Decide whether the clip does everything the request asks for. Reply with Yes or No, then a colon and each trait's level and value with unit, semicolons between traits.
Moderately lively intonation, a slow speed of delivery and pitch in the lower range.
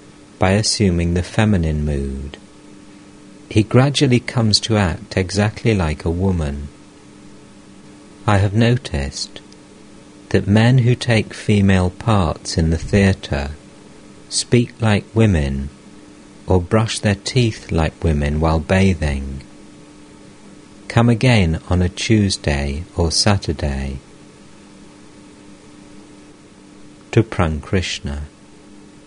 Yes: average, 4.0 semitones; slow, 95 wpm; low, 100 Hz